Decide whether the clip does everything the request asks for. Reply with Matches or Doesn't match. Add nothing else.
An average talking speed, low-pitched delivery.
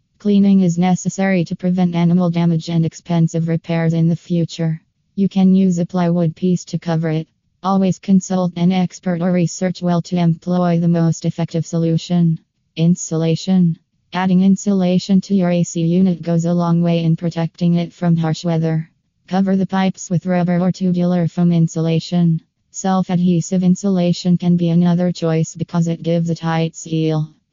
Doesn't match